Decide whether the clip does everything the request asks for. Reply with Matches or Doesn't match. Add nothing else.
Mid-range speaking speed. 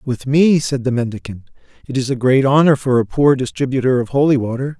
Doesn't match